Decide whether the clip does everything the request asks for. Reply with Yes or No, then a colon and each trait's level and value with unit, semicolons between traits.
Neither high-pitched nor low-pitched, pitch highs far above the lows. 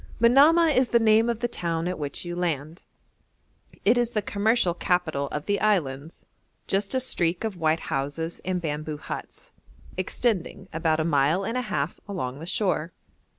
Yes: medium, 180 Hz; wide, 5.7 semitones